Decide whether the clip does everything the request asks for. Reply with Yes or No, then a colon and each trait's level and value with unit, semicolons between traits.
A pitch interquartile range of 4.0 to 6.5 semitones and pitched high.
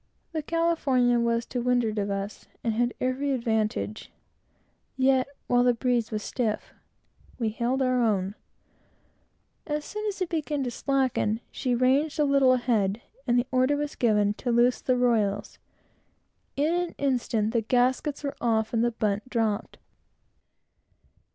No: average, 3.3 semitones; high, 245 Hz